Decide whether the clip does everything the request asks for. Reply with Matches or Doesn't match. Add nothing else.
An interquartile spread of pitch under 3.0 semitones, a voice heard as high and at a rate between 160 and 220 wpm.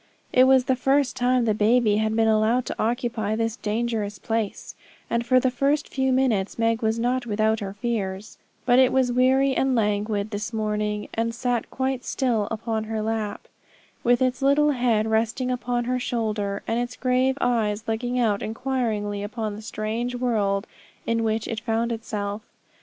Matches